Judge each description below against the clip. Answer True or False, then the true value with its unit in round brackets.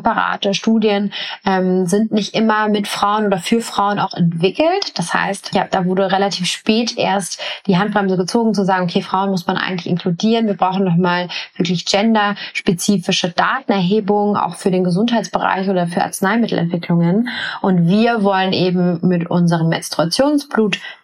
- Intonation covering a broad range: False (2.4 semitones)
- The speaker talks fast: False (150 wpm)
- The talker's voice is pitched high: True (195 Hz)